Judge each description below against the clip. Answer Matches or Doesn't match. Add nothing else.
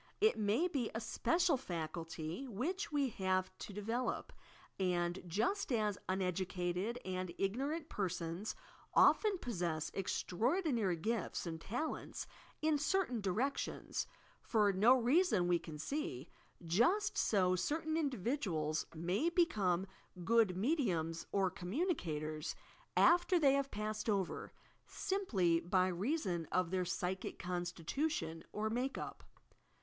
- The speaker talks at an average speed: Doesn't match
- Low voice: Doesn't match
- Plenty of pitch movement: Matches